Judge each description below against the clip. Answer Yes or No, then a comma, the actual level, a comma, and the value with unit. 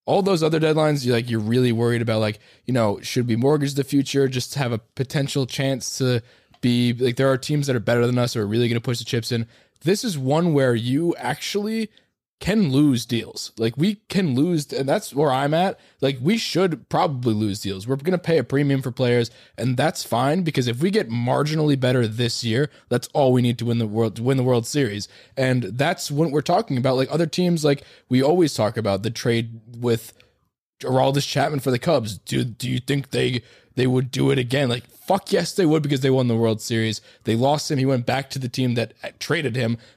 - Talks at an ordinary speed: No, fast, 235 wpm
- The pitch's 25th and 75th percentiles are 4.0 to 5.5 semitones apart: No, average, 3.5 semitones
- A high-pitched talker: No, low, 130 Hz